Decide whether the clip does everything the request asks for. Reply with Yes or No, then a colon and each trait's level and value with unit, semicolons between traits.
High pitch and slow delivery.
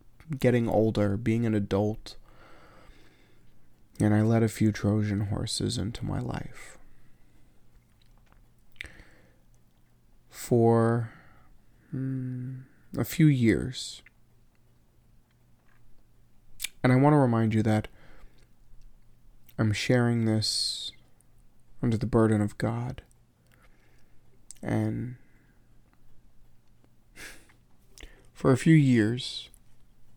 No: low, 110 Hz; slow, 80 wpm